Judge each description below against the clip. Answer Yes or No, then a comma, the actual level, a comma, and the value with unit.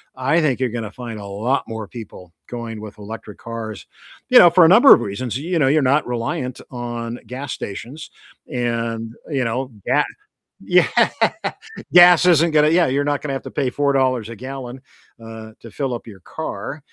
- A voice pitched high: No, low, 125 Hz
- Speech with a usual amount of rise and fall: Yes, average, 4.0 semitones